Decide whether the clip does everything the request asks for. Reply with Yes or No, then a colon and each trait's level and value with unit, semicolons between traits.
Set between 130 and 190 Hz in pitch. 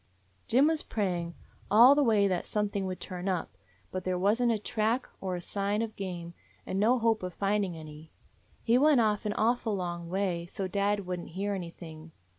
No: high, 200 Hz